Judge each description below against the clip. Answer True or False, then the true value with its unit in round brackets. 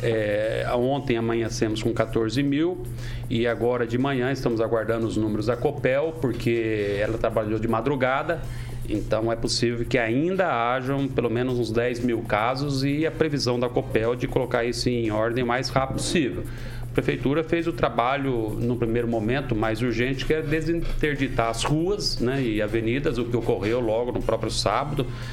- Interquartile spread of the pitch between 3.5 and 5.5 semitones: False (2.7 semitones)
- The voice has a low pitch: True (120 Hz)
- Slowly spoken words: False (170 wpm)